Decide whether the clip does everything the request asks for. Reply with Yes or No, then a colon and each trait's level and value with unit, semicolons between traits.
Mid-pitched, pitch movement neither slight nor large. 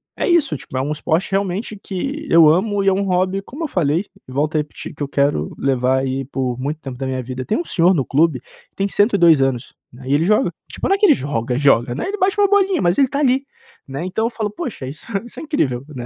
No: medium, 165 Hz; wide, 8.1 semitones